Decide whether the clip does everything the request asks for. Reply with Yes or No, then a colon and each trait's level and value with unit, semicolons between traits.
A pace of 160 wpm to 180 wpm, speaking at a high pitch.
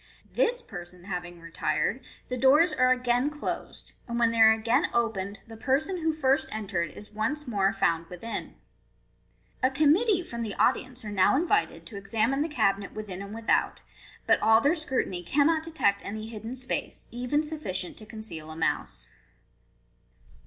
Yes: average, 165 wpm; high, 230 Hz